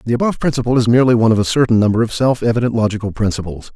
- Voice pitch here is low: Yes, low, 115 Hz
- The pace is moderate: No, fast, 240 wpm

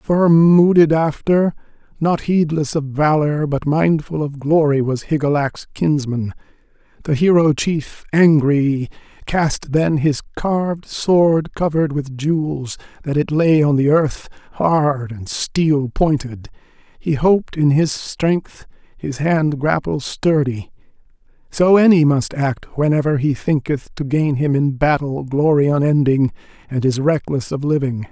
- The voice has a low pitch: No, medium, 150 Hz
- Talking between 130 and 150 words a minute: Yes, slow, 135 wpm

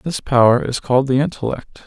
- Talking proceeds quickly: No, average, 195 wpm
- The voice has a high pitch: No, low, 135 Hz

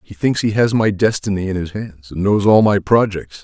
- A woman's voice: No, male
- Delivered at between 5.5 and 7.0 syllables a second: No, 5.1 syllables/s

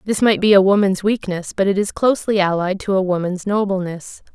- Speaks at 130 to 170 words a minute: No, fast, 205 wpm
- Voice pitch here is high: Yes, high, 195 Hz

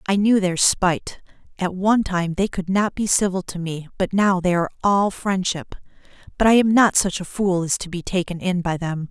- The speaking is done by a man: No, female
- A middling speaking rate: No, fast, 225 wpm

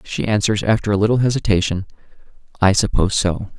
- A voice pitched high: No, low, 100 Hz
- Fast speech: No, average, 150 wpm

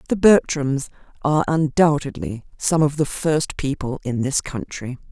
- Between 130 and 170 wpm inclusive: Yes, average, 140 wpm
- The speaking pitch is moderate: Yes, medium, 145 Hz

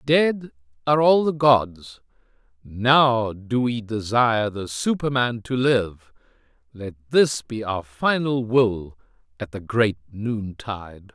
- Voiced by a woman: No, male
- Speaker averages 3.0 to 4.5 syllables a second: Yes, 3.5 syllables/s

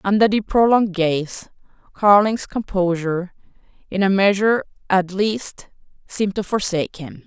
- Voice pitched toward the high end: Yes, high, 195 Hz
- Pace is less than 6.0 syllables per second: Yes, 4.8 syllables/s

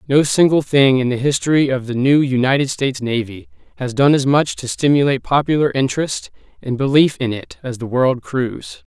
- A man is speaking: Yes, male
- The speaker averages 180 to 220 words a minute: Yes, average, 190 wpm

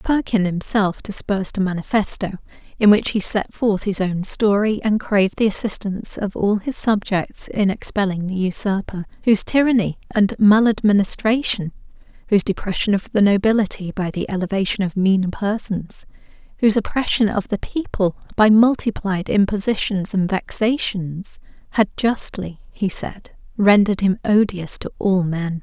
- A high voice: Yes, high, 200 Hz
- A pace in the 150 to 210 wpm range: No, average, 140 wpm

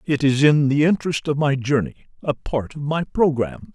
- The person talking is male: Yes, male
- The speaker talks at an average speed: Yes, average, 190 wpm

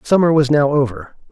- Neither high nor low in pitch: Yes, medium, 145 Hz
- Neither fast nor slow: Yes, average, 185 wpm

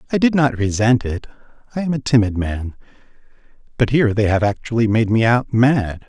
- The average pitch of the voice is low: Yes, low, 115 Hz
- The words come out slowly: No, average, 190 wpm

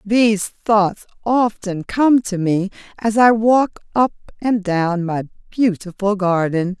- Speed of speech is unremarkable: No, slow, 130 wpm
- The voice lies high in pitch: Yes, high, 205 Hz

